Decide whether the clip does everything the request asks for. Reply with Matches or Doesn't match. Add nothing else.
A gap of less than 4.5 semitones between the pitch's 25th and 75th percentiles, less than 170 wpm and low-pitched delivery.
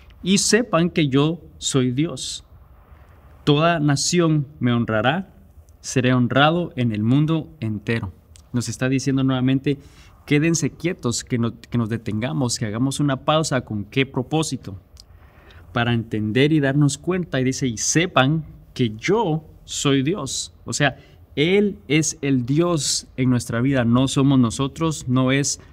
Doesn't match